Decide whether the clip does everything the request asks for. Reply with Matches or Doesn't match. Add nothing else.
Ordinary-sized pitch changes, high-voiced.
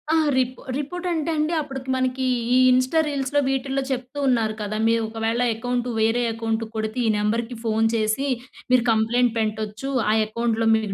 Matches